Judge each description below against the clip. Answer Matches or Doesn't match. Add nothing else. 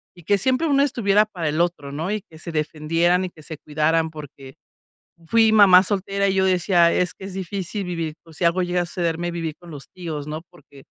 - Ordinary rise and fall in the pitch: Matches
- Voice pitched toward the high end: Doesn't match